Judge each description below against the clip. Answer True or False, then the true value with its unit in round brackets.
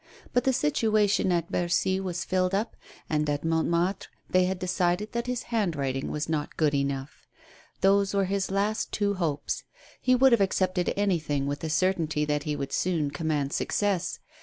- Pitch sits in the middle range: True (180 Hz)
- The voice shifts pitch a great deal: False (4.7 semitones)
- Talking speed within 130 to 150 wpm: False (170 wpm)